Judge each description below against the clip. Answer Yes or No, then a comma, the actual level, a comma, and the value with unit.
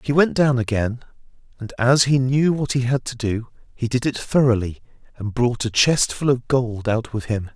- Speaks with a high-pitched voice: No, low, 125 Hz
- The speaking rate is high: Yes, fast, 215 wpm